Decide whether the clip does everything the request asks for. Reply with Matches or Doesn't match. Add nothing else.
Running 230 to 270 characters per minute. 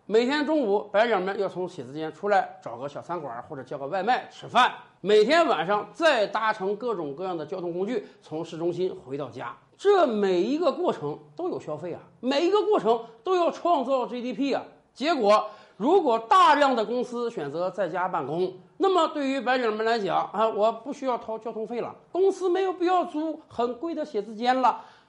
Doesn't match